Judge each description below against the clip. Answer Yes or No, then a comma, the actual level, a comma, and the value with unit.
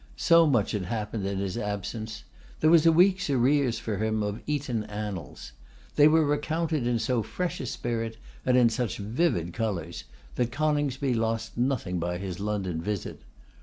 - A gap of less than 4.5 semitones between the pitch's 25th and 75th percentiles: No, wide, 5.6 semitones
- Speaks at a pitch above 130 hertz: No, low, 115 Hz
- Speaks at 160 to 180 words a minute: Yes, average, 165 wpm